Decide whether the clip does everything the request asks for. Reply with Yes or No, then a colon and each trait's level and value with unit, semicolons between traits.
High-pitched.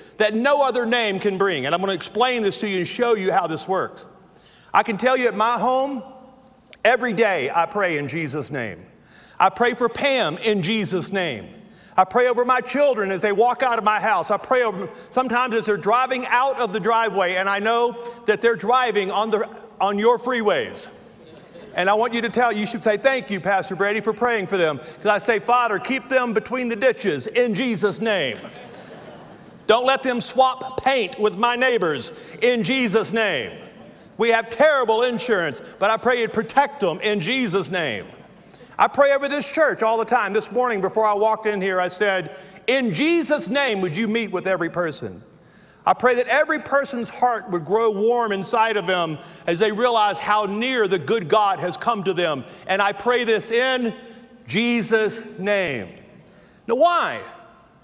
Yes: high, 225 Hz